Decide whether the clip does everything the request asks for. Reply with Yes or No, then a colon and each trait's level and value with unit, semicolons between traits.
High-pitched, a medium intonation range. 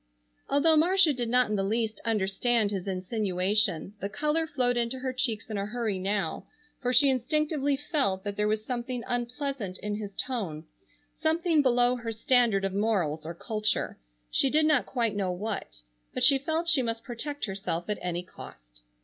Yes: high, 230 Hz; average, 4.9 semitones